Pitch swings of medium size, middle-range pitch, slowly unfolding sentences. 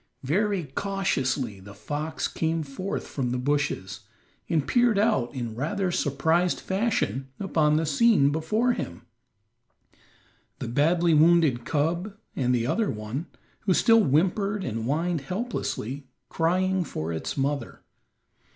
No: wide, 6.1 semitones; medium, 155 Hz; slow, 125 wpm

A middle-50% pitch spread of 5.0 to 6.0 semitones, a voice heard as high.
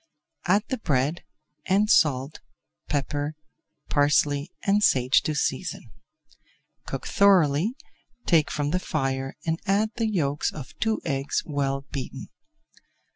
No: wide, 5.4 semitones; medium, 150 Hz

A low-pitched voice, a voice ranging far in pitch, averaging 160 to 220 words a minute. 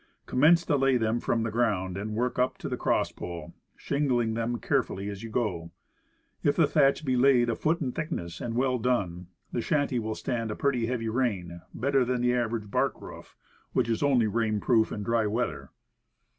No: low, 120 Hz; average, 3.2 semitones; average, 195 wpm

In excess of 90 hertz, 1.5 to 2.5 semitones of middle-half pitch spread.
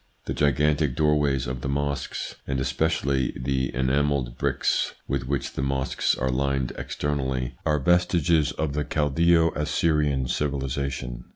No: very low, 70 Hz; narrow, 2.2 semitones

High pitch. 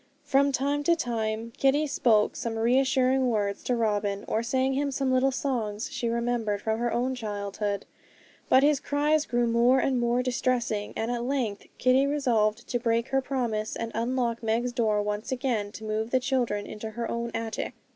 Yes: high, 240 Hz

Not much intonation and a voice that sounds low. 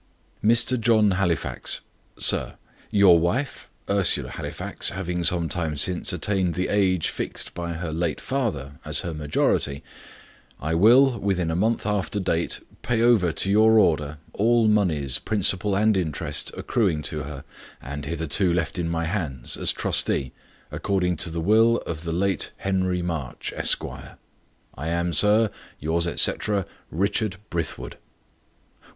No: average, 4.1 semitones; very low, 90 Hz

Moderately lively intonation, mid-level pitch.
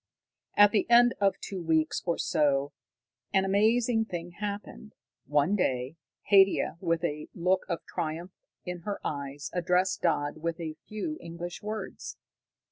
Yes: average, 4.2 semitones; medium, 180 Hz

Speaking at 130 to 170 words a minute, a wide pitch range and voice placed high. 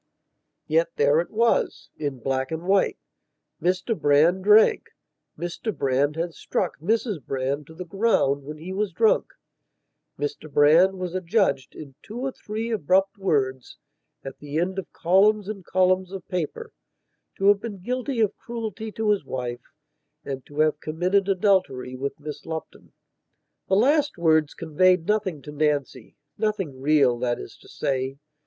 No: average, 150 wpm; wide, 6.1 semitones; medium, 175 Hz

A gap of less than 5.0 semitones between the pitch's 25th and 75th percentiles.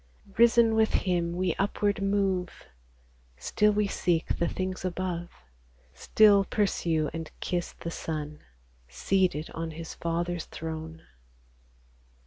Yes: average, 3.3 semitones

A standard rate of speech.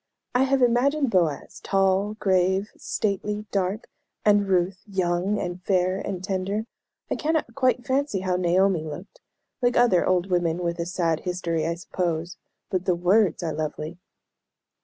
Yes: average, 150 wpm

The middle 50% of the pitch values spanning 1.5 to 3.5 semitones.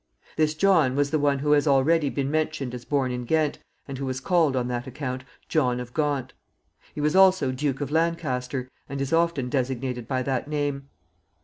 Yes: average, 3.0 semitones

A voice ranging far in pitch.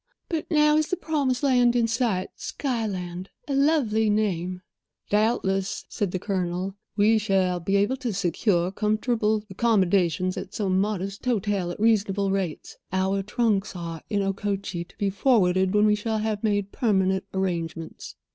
No: average, 3.0 semitones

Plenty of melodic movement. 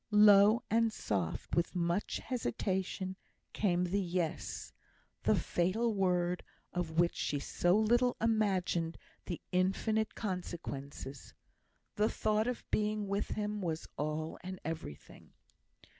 No: average, 3.8 semitones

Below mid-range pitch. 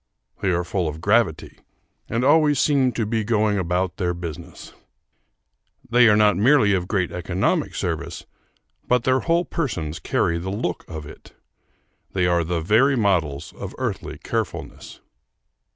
Yes: low, 100 Hz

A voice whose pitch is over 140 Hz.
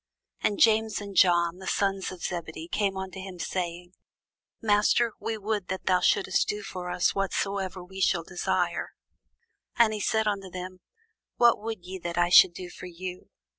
Yes: high, 190 Hz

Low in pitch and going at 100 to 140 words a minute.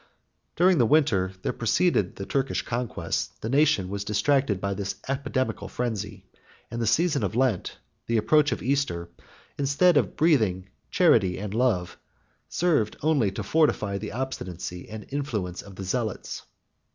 No: low, 115 Hz; average, 150 wpm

